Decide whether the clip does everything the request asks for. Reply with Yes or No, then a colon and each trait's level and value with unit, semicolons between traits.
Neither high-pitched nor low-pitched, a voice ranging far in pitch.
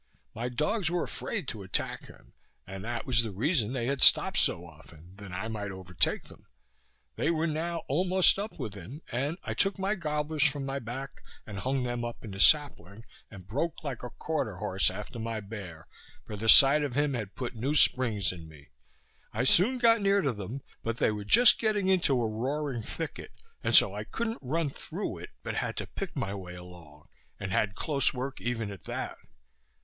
No: low, 120 Hz; wide, 7.0 semitones